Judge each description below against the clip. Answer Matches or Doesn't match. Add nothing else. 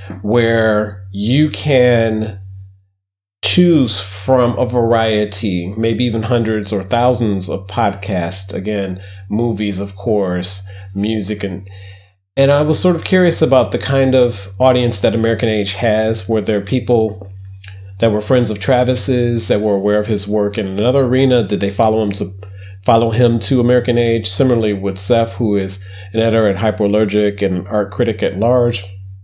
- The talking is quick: Doesn't match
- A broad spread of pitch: Doesn't match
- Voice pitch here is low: Matches